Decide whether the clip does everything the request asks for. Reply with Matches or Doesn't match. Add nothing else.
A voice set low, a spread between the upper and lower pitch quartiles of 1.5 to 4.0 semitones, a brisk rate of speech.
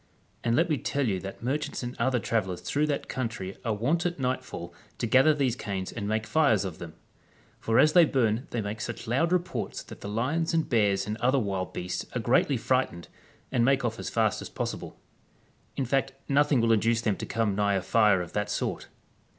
Doesn't match